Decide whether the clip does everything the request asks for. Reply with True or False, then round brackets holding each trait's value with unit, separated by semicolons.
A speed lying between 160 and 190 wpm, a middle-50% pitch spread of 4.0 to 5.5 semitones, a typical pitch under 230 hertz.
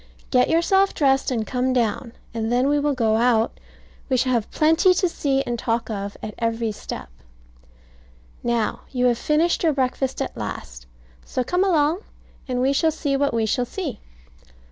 False (175 wpm; 4.3 semitones; 255 Hz)